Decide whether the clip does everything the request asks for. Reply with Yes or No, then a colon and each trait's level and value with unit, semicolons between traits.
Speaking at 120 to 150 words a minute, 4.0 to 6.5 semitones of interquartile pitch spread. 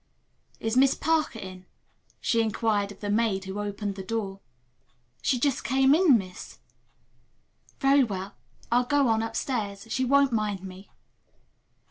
Yes: average, 140 wpm; average, 4.7 semitones